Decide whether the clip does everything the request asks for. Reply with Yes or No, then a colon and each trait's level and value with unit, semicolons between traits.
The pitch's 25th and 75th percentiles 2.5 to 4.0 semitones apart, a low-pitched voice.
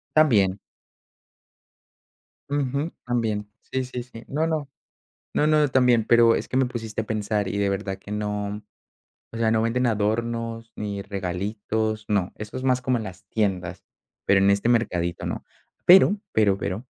Yes: average, 3.5 semitones; low, 110 Hz